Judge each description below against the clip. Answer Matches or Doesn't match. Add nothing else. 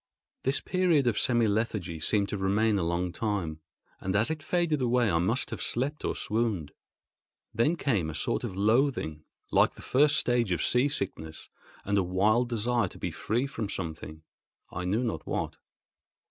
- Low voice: Matches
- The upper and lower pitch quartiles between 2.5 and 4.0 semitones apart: Doesn't match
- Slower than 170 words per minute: Doesn't match